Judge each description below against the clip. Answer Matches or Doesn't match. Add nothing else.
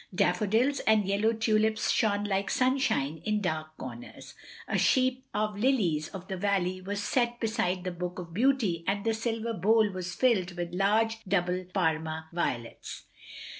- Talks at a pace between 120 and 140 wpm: Doesn't match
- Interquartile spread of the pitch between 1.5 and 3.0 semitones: Doesn't match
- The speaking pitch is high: Matches